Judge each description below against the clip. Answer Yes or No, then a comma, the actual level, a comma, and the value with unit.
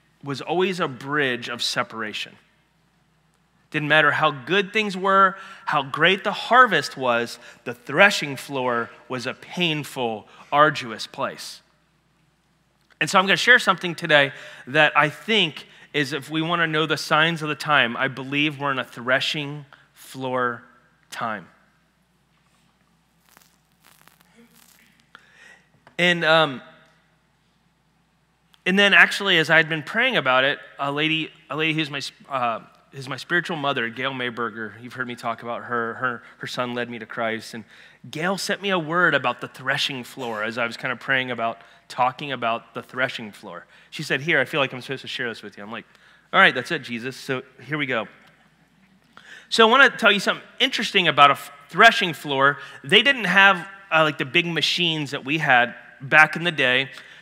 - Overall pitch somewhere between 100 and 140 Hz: No, medium, 155 Hz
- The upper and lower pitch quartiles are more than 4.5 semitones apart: Yes, average, 5.2 semitones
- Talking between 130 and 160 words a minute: No, average, 175 wpm